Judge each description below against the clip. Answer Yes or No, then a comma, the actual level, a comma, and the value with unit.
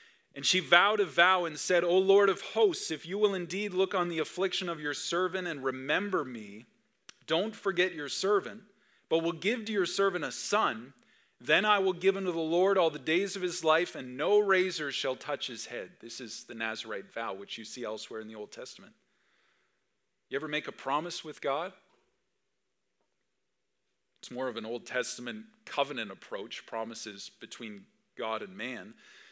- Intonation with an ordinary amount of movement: No, wide, 7.5 semitones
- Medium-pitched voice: Yes, medium, 170 Hz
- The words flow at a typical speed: Yes, average, 185 wpm